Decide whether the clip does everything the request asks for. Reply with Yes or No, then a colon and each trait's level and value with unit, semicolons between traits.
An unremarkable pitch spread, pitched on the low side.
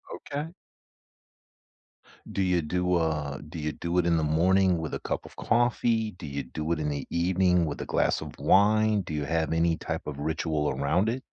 Yes: average, 3.6 semitones; very low, 85 Hz